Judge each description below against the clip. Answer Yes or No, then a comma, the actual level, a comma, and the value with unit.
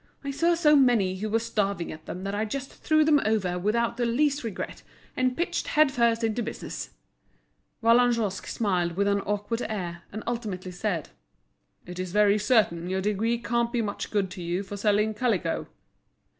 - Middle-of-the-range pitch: No, high, 215 Hz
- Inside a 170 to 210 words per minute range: Yes, average, 175 wpm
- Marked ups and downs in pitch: No, average, 3.8 semitones